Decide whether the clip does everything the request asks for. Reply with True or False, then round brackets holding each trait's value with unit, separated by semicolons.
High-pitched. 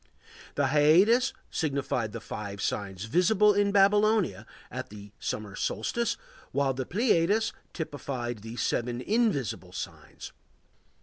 False (140 Hz)